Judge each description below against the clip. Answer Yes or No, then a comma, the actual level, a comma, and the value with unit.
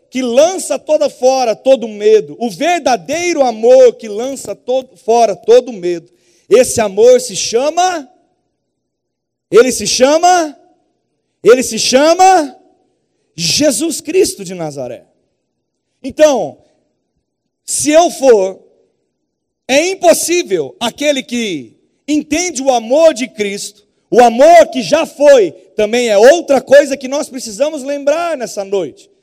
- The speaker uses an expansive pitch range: Yes, wide, 5.7 semitones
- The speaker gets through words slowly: Yes, slow, 115 wpm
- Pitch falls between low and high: No, very high, 275 Hz